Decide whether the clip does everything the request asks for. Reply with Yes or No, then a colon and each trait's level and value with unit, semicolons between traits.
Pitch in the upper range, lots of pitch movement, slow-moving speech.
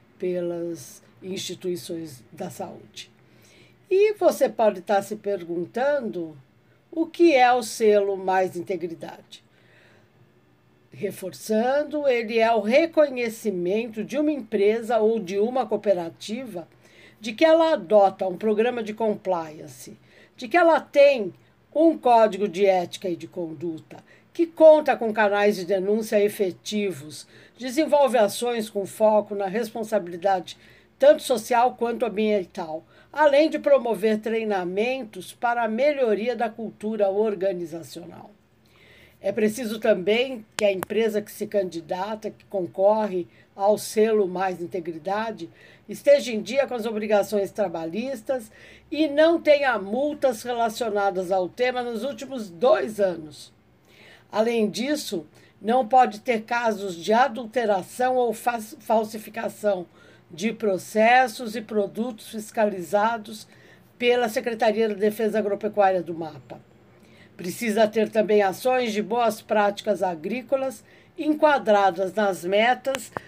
No: high, 215 Hz; average, 4.1 semitones; slow, 115 wpm